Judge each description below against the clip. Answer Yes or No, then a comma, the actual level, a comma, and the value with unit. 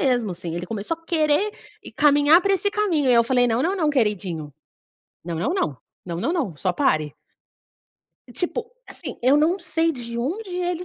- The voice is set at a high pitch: Yes, very high, 280 Hz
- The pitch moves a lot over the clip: Yes, wide, 8.5 semitones